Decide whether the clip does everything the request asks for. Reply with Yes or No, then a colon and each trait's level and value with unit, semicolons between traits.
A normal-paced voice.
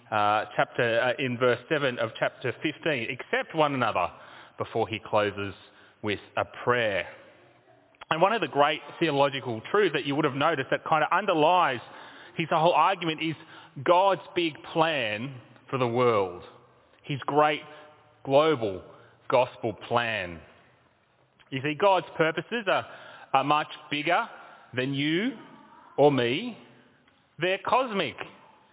No: slow, 130 wpm